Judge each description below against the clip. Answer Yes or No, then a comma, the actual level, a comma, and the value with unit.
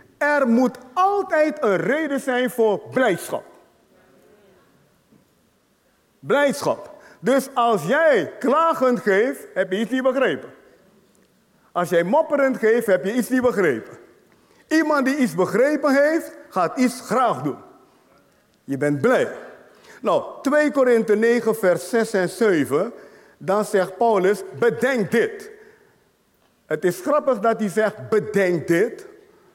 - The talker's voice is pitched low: No, very high, 250 Hz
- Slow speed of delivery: Yes, slow, 125 wpm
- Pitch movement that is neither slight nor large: No, wide, 5.8 semitones